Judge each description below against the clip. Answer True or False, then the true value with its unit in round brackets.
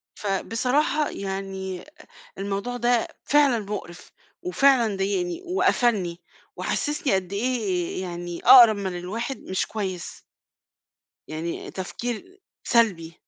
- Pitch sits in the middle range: False (200 Hz)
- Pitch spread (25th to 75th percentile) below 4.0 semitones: False (4.8 semitones)